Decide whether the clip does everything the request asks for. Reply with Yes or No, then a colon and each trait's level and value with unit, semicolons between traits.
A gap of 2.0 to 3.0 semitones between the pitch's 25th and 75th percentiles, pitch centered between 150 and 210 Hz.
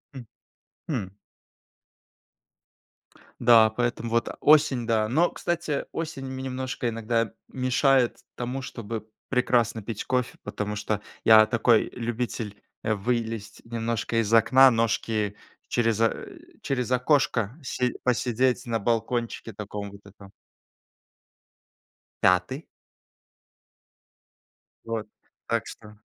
No: narrow, 2.5 semitones; low, 115 Hz